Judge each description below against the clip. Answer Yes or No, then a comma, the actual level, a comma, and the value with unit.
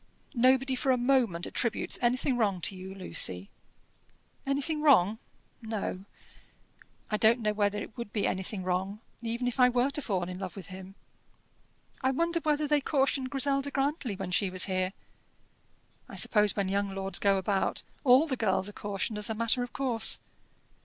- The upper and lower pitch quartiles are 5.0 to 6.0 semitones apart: Yes, average, 5.3 semitones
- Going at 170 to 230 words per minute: Yes, average, 175 wpm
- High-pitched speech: Yes, high, 225 Hz